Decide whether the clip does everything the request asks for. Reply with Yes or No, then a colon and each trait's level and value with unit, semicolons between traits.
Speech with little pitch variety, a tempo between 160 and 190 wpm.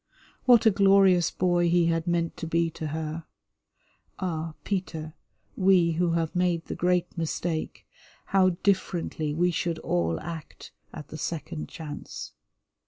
No: narrow, 2.1 semitones; average, 140 wpm